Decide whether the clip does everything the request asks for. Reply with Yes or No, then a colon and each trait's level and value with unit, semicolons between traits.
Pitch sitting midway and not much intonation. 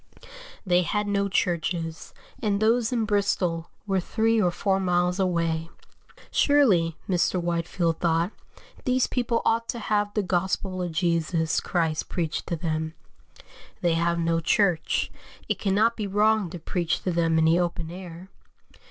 No: medium, 180 Hz; average, 3.6 semitones